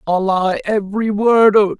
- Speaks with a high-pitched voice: Yes, high, 205 Hz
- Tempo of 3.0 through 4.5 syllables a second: Yes, 4.4 syllables/s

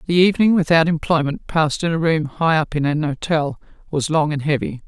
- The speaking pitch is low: No, medium, 155 Hz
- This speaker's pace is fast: Yes, fast, 210 wpm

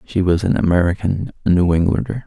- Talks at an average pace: Yes, average, 185 wpm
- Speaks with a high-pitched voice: No, very low, 90 Hz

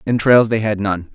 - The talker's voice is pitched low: Yes, low, 110 Hz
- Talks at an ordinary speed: No, fast, 210 wpm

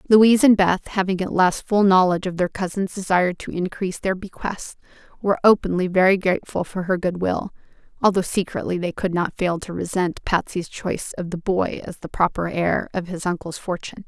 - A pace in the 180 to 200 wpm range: Yes, average, 190 wpm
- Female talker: Yes, female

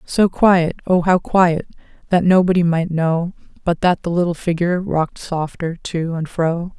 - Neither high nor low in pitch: Yes, medium, 175 Hz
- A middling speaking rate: Yes, average, 170 wpm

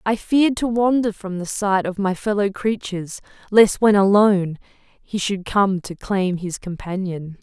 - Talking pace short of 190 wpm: Yes, average, 170 wpm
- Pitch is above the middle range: Yes, high, 200 Hz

